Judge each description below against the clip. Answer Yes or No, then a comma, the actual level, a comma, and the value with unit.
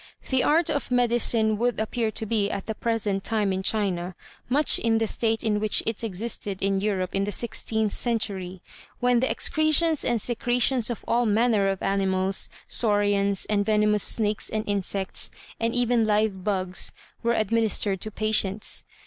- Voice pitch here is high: Yes, high, 215 Hz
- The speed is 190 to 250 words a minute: No, average, 165 wpm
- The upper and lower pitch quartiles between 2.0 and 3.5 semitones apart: Yes, average, 2.9 semitones